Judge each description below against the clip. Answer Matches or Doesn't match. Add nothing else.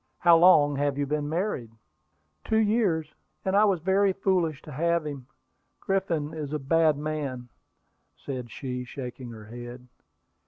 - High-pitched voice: Doesn't match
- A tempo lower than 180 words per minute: Matches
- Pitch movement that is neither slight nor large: Matches